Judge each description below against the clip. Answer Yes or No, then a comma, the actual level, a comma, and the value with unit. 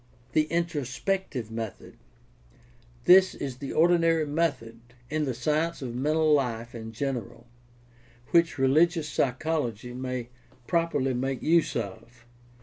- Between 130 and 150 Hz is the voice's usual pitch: Yes, low, 135 Hz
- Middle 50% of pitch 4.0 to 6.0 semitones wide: Yes, average, 5.0 semitones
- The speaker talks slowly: Yes, slow, 125 wpm